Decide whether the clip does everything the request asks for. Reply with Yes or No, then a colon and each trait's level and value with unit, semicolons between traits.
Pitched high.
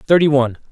No: medium, 140 Hz